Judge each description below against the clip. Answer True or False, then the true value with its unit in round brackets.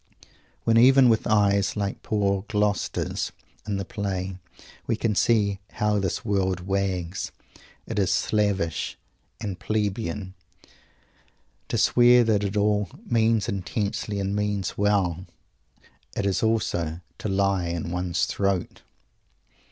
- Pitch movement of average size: False (2.0 semitones)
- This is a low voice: True (100 Hz)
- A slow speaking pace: True (120 wpm)